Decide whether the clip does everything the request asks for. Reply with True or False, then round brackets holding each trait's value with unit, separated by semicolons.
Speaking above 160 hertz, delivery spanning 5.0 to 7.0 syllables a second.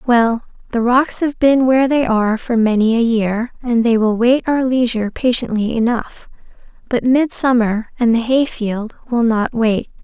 False (235 Hz; 4.5 syllables/s)